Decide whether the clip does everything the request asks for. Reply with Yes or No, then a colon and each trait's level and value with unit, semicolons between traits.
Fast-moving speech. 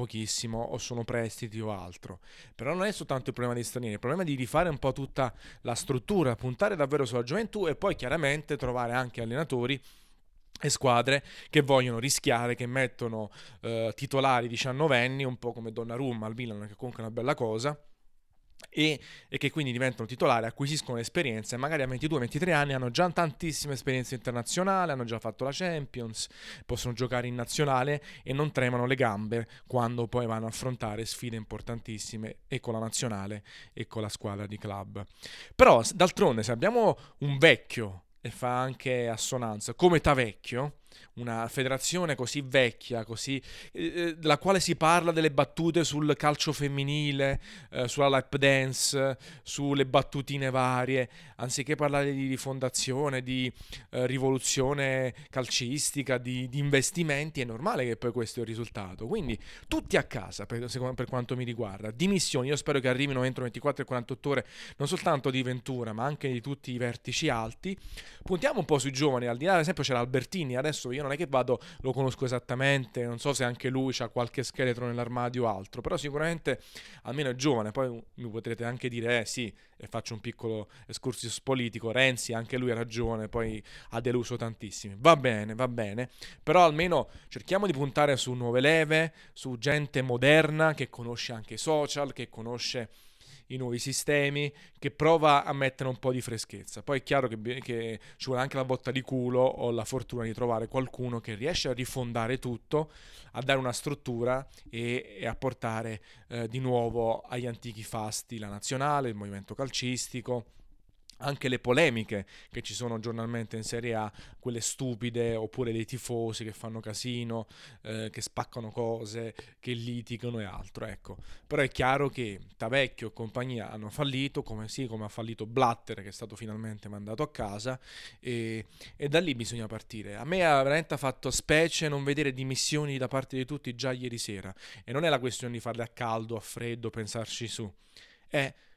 Yes: fast, 175 wpm